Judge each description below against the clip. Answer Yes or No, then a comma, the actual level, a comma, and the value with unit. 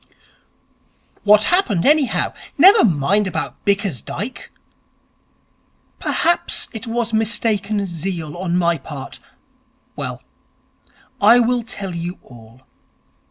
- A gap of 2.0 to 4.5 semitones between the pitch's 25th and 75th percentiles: No, average, 5.2 semitones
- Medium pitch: No, high, 200 Hz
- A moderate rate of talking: No, slow, 95 wpm